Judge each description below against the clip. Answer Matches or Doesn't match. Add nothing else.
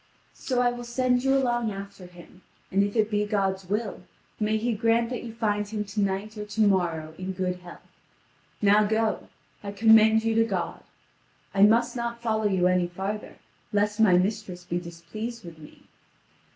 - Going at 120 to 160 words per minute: Doesn't match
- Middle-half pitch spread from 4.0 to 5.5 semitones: Doesn't match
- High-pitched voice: Matches